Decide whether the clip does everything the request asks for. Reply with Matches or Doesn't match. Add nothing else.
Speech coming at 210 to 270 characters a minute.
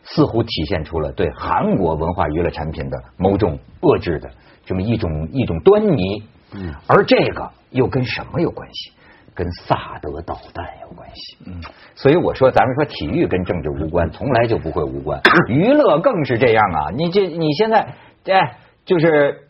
Matches